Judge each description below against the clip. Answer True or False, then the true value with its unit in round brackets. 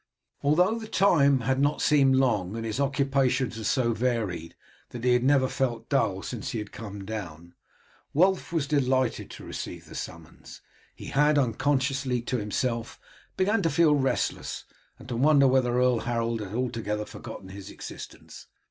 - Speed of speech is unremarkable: True (165 wpm)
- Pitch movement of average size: True (3.7 semitones)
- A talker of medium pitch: False (125 Hz)